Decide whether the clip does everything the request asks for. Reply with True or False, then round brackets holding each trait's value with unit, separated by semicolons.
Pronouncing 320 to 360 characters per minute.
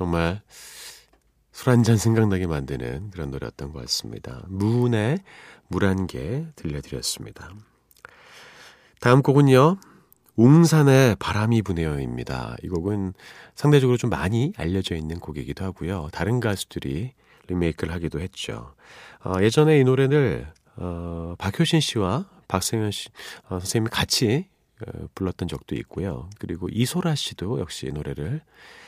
False (285 characters per minute)